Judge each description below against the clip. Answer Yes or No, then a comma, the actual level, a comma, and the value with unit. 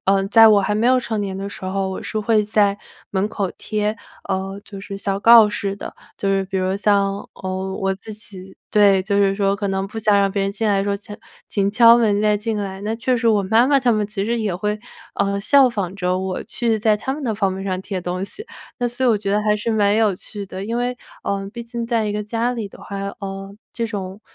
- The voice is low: No, high, 205 Hz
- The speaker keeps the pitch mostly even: Yes, narrow, 2.2 semitones